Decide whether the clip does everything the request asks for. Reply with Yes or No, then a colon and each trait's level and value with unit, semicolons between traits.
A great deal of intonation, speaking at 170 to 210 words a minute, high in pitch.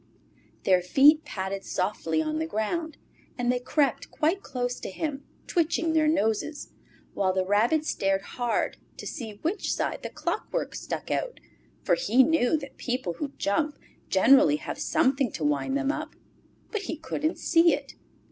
No: wide, 7.9 semitones; average, 160 wpm; very high, 265 Hz